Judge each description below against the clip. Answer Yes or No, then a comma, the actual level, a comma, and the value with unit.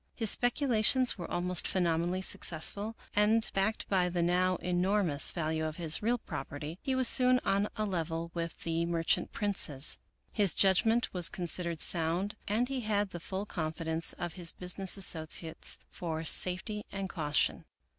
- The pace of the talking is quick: No, average, 155 wpm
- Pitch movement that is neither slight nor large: Yes, average, 3.9 semitones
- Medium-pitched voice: Yes, medium, 180 Hz